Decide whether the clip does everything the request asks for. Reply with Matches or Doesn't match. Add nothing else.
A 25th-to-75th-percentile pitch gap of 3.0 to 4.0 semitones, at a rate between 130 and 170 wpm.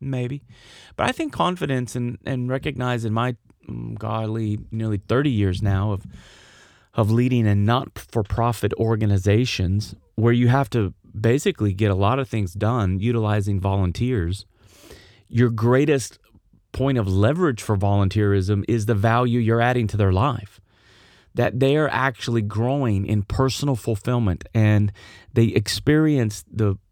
Matches